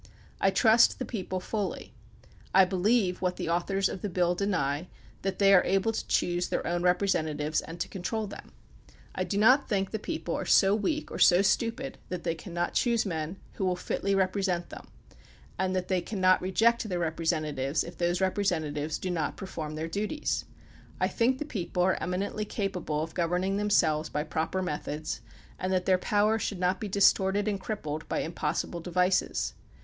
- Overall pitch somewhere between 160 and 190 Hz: Yes, medium, 185 Hz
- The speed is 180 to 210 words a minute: Yes, average, 185 wpm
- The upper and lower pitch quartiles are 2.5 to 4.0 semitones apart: Yes, average, 2.8 semitones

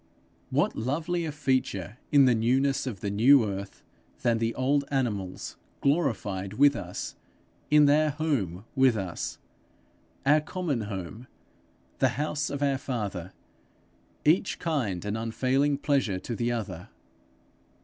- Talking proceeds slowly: Yes, slow, 130 wpm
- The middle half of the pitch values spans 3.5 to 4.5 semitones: No, wide, 5.6 semitones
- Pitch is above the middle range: No, low, 130 Hz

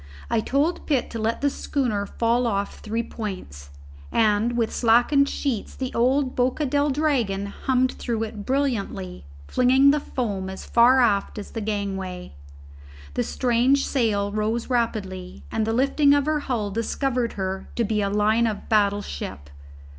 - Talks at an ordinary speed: Yes, average, 160 wpm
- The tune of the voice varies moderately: Yes, average, 4.2 semitones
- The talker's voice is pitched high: Yes, high, 230 Hz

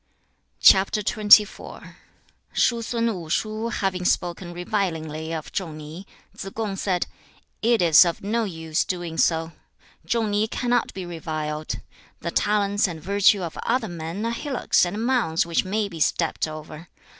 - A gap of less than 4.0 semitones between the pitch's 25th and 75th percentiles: No, average, 4.8 semitones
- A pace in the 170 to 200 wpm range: No, average, 145 wpm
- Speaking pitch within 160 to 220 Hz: Yes, medium, 185 Hz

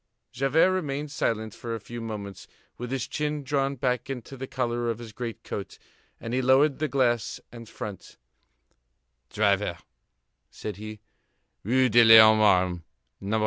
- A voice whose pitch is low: Yes, low, 120 Hz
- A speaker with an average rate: Yes, average, 150 wpm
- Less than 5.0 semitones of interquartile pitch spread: Yes, average, 3.8 semitones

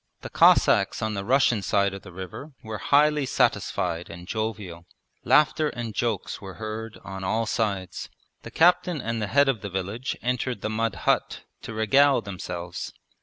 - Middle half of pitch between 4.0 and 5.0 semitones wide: Yes, average, 4.6 semitones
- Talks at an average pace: Yes, average, 170 wpm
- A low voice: Yes, low, 110 Hz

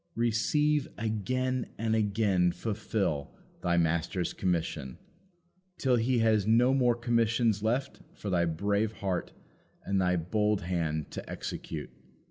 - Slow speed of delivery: Yes, slow, 120 wpm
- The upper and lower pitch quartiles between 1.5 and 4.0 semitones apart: No, average, 4.5 semitones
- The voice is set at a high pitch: No, low, 105 Hz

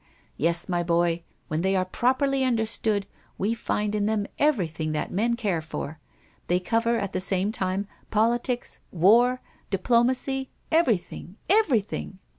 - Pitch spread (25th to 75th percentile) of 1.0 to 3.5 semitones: No, average, 4.8 semitones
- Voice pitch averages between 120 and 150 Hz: No, high, 210 Hz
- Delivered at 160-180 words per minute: No, slow, 135 wpm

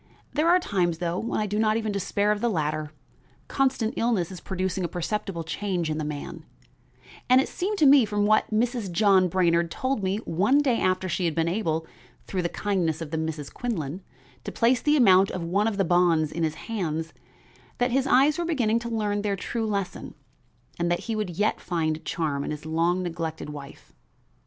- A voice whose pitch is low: No, high, 190 Hz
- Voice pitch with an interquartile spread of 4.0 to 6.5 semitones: Yes, average, 5.1 semitones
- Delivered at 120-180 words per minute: No, fast, 205 wpm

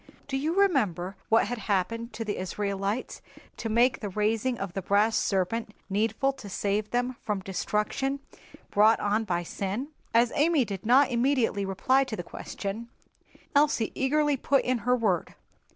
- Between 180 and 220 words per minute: No, average, 160 wpm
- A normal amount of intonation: Yes, average, 4.3 semitones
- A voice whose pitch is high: Yes, high, 225 Hz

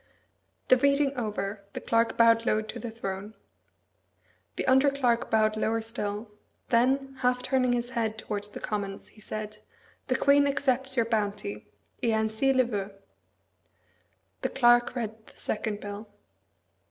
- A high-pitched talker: Yes, high, 230 Hz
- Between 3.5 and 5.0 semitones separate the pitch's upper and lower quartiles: No, average, 3.1 semitones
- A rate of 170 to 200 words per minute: No, average, 145 wpm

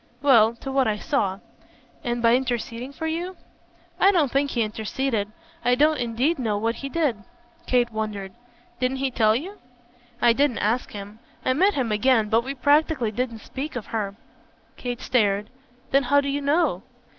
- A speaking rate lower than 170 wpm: No, average, 175 wpm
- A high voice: Yes, high, 245 Hz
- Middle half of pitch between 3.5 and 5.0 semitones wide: Yes, average, 4.1 semitones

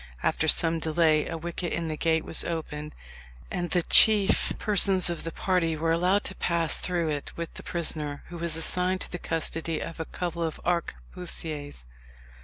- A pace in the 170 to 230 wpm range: Yes, average, 180 wpm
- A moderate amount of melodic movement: No, narrow, 1.9 semitones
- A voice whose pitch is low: No, medium, 165 Hz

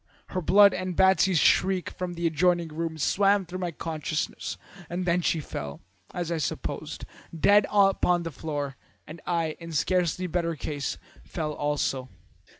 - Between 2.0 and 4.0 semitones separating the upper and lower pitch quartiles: Yes, average, 2.8 semitones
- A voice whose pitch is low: No, medium, 170 Hz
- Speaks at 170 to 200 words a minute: No, average, 150 wpm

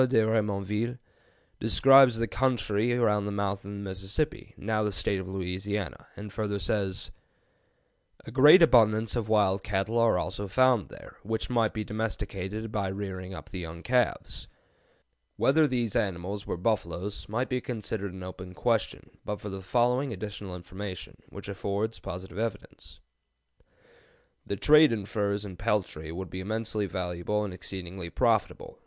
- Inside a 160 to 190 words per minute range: No, average, 150 wpm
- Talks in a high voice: No, low, 105 Hz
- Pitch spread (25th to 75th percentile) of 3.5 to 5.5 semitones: No, average, 2.9 semitones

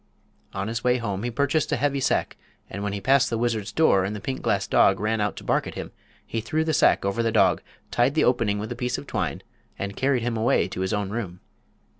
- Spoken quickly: Yes, fast, 250 wpm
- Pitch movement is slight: No, average, 3.6 semitones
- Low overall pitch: Yes, low, 115 Hz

